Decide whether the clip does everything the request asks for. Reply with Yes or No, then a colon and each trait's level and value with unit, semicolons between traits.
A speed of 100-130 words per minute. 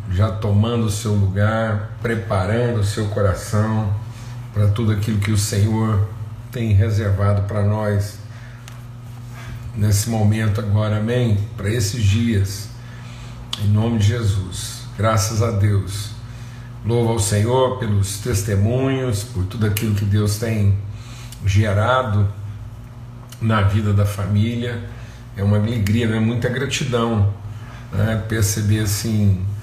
Yes: slow, 120 wpm